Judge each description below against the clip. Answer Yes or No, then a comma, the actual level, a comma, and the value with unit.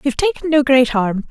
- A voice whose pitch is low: No, very high, 270 Hz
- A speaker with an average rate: No, fast, 230 wpm